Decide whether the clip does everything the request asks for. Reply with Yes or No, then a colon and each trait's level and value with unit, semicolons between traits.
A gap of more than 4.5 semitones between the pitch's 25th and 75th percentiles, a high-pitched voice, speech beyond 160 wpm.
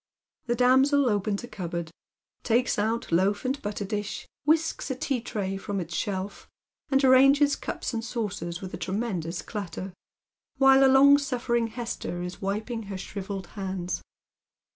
No: average, 5.0 semitones; high, 215 Hz; average, 145 wpm